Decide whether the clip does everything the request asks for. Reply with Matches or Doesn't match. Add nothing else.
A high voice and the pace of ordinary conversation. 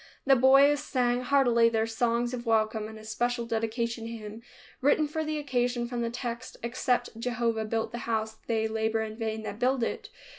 Matches